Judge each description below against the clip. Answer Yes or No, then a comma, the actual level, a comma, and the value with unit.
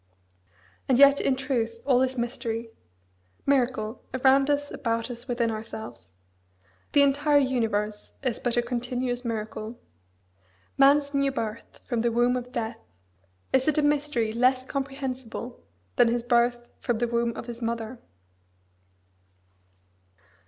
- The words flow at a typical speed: No, slow, 130 wpm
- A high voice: Yes, high, 245 Hz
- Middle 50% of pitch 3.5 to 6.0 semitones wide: No, narrow, 2.6 semitones